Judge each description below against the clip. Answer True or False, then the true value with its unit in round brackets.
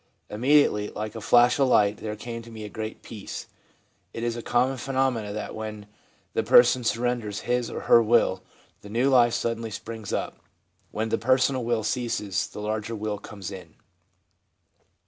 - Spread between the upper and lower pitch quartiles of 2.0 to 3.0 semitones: True (2.4 semitones)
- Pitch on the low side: True (115 Hz)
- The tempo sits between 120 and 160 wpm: False (175 wpm)